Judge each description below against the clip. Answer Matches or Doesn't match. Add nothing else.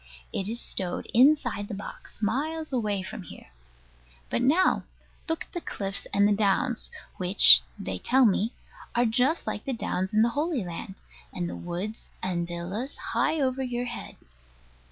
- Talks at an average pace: Matches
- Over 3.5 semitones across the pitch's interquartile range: Matches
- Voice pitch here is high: Matches